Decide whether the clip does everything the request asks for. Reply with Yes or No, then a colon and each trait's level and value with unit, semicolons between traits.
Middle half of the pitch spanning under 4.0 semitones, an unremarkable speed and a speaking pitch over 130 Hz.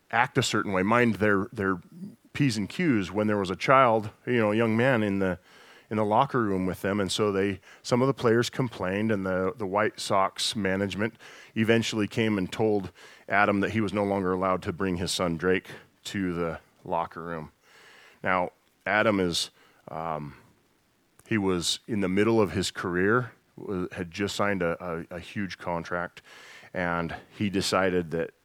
No: average, 3.2 semitones; average, 180 wpm; low, 100 Hz